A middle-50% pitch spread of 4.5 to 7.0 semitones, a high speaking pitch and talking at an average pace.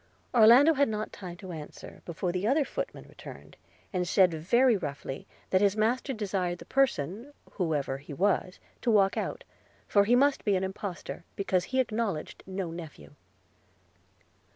Yes: average, 5.0 semitones; high, 195 Hz; average, 160 wpm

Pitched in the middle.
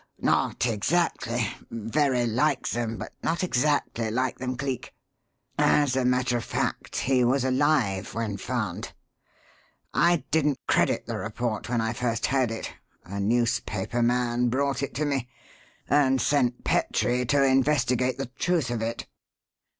No: low, 125 Hz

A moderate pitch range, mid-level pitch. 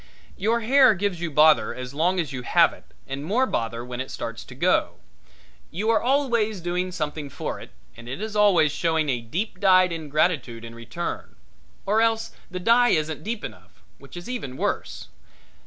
No: wide, 7.3 semitones; medium, 175 Hz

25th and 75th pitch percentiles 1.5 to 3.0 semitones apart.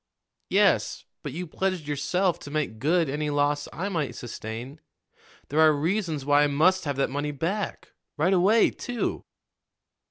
No: average, 4.0 semitones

